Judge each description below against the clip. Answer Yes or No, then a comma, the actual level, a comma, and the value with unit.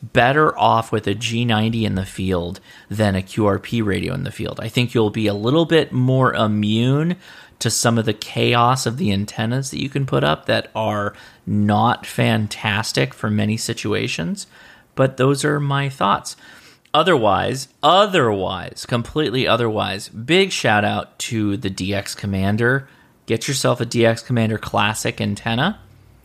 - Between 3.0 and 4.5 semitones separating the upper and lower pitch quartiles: Yes, average, 3.3 semitones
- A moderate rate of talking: Yes, average, 155 wpm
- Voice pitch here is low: Yes, low, 115 Hz